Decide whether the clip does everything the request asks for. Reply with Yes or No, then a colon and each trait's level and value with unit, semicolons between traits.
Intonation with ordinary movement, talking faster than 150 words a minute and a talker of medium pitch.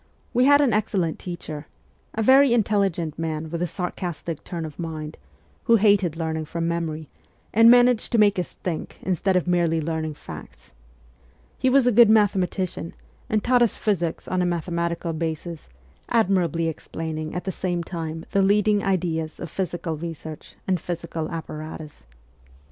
Yes: average, 4.0 semitones; average, 160 wpm; medium, 175 Hz